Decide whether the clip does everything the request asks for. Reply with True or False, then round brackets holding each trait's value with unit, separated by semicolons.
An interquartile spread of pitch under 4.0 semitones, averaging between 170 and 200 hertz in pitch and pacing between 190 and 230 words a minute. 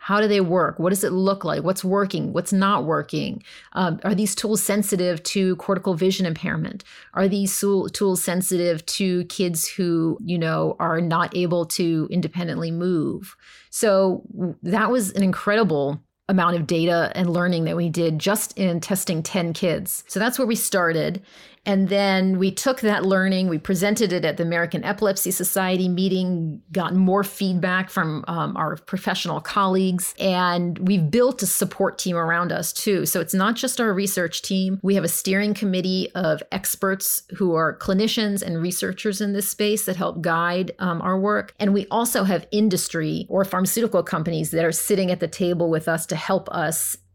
False (2.4 semitones; 185 Hz; 180 wpm)